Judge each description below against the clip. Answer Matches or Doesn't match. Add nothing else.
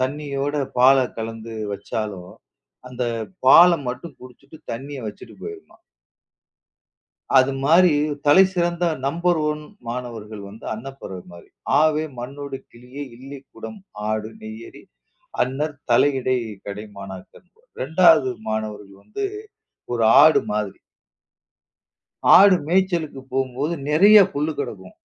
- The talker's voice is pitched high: Doesn't match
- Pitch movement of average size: Doesn't match